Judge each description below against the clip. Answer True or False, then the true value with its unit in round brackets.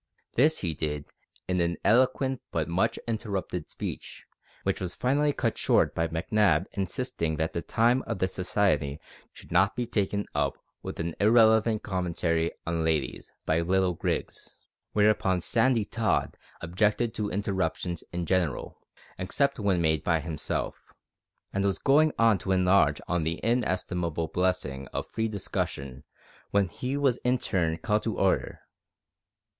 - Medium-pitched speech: False (95 Hz)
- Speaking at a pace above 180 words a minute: False (145 wpm)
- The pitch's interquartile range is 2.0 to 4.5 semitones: False (4.9 semitones)